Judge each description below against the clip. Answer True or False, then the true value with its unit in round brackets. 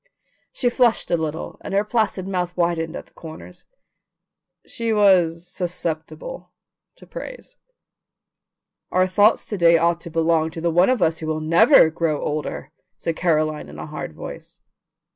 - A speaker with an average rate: True (160 wpm)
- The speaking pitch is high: False (170 Hz)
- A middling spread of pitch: True (3.8 semitones)